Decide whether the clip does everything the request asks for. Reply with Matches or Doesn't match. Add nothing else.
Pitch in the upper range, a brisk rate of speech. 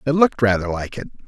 Doesn't match